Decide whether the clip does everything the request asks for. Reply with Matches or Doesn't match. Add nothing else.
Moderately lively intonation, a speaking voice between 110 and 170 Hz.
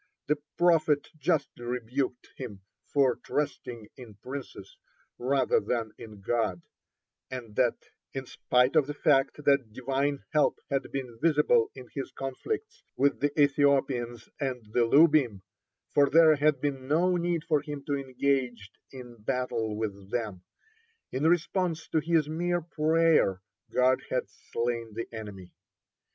Matches